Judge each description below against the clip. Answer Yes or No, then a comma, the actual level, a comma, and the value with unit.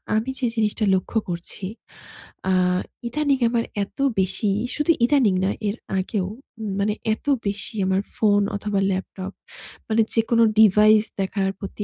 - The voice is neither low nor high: No, high, 210 Hz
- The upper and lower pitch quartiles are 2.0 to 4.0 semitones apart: Yes, average, 2.7 semitones